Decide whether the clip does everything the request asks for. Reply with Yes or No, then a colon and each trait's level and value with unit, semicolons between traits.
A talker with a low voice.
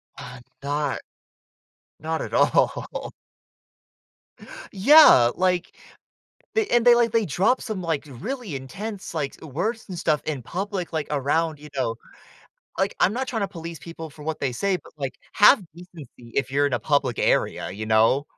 No: medium, 160 Hz